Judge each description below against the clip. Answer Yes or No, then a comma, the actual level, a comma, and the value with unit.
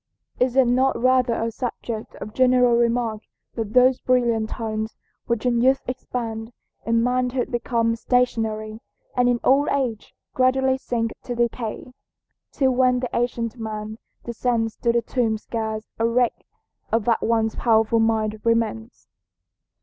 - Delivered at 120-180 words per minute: Yes, average, 140 wpm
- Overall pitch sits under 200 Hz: No, high, 235 Hz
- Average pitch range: No, narrow, 2.0 semitones